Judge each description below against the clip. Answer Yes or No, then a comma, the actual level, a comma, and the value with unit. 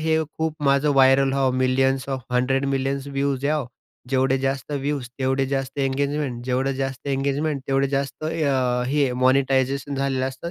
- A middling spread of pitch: No, narrow, 1.0 semitones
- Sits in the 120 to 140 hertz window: Yes, low, 135 Hz